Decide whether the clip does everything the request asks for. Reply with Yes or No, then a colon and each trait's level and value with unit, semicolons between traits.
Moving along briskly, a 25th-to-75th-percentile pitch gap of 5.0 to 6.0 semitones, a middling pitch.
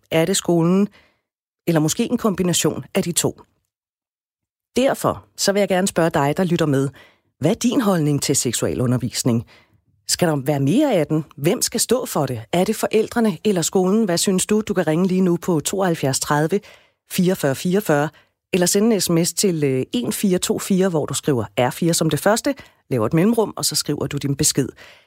No: average, 185 wpm; wide, 5.4 semitones; medium, 170 Hz